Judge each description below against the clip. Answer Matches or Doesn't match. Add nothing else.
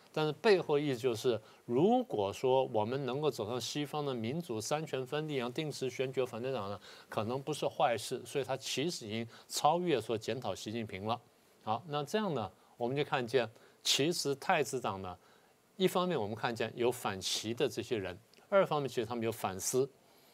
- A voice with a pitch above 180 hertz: Doesn't match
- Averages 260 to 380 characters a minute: Matches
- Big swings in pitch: Doesn't match